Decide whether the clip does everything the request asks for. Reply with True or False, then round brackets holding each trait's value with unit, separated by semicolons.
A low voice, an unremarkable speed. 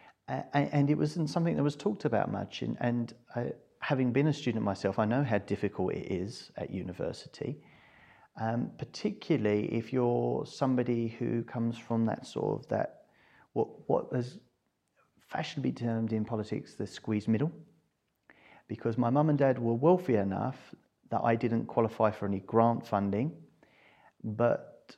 True (120 Hz; 155 wpm)